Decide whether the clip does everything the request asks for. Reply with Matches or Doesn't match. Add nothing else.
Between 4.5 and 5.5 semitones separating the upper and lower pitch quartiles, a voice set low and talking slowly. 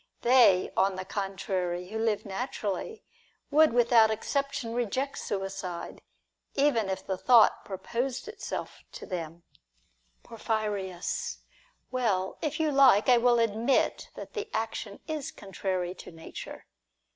Doesn't match